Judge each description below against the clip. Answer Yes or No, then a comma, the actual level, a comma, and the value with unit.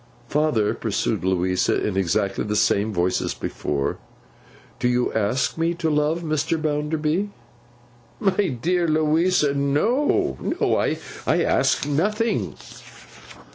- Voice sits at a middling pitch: Yes, medium, 150 Hz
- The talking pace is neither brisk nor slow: No, slow, 115 wpm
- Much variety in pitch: Yes, wide, 7.6 semitones